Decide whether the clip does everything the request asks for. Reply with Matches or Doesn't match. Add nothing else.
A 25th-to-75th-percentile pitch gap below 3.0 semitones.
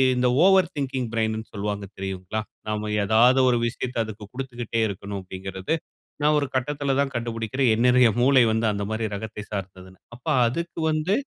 Doesn't match